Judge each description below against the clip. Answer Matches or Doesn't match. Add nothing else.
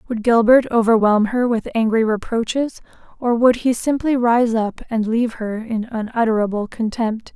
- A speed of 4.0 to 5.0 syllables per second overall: Matches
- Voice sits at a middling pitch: Doesn't match